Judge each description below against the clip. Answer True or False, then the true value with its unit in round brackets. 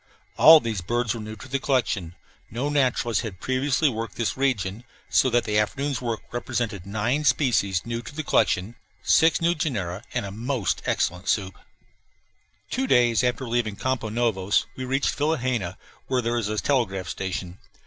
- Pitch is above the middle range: False (120 Hz)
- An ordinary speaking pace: True (170 wpm)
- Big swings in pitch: False (4.1 semitones)